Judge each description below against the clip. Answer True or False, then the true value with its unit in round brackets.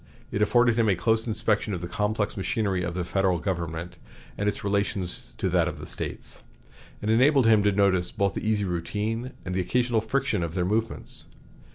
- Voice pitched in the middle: False (105 Hz)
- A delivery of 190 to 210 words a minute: True (195 wpm)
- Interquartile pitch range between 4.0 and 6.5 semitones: False (3.3 semitones)